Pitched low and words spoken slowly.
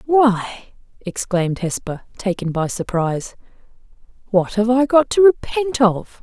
No: high, 215 Hz; slow, 125 wpm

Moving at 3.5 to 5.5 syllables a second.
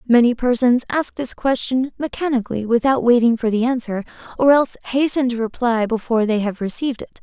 No: 5.8 syllables/s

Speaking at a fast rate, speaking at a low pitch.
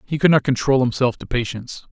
Yes: fast, 215 wpm; low, 130 Hz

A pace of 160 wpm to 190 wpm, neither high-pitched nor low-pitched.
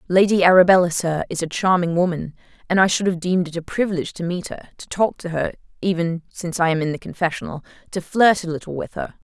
No: average, 200 wpm; medium, 175 Hz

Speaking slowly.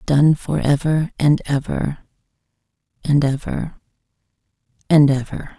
Yes: slow, 95 wpm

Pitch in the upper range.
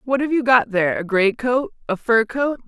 Yes: high, 240 Hz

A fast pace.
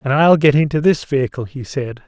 Yes: fast, 230 wpm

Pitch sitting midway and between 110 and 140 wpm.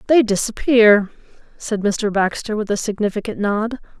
No: high, 210 Hz; slow, 135 wpm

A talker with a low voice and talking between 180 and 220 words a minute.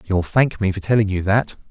No: low, 100 Hz; fast, 245 wpm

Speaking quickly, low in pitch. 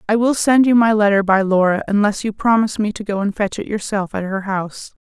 No: fast, 250 wpm; high, 205 Hz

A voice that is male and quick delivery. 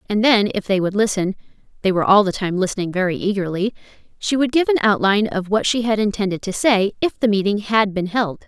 No: female; fast, 210 wpm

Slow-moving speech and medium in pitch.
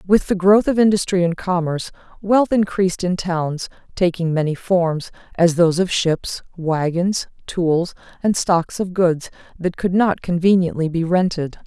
No: average, 155 wpm; medium, 180 Hz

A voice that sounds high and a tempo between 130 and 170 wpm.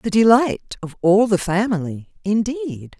Yes: high, 205 Hz; average, 140 wpm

